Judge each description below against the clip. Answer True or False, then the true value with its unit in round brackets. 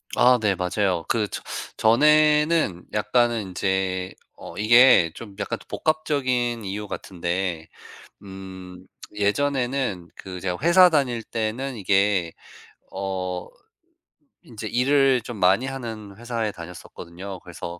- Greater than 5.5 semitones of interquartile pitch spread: False (5.1 semitones)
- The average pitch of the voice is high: False (105 Hz)